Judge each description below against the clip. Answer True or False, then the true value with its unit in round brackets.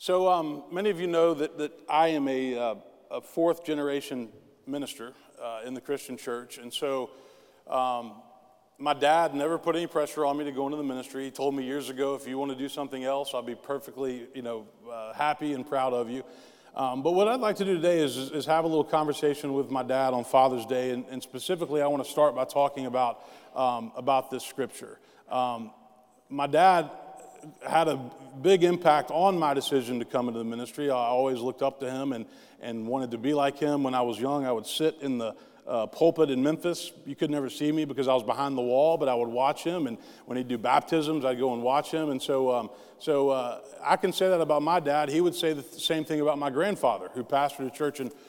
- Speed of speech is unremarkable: False (235 wpm)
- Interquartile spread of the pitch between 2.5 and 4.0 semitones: True (3.1 semitones)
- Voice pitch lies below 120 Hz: False (140 Hz)